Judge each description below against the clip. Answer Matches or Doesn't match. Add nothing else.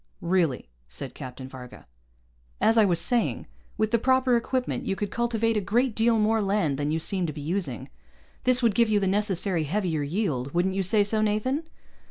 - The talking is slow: Doesn't match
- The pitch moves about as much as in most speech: Doesn't match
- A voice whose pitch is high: Matches